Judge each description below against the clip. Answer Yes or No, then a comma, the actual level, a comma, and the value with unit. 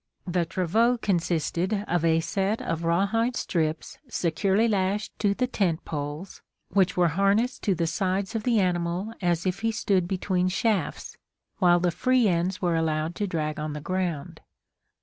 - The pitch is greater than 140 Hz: Yes, medium, 185 Hz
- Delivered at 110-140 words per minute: No, average, 165 wpm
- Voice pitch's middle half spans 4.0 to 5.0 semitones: No, average, 3.3 semitones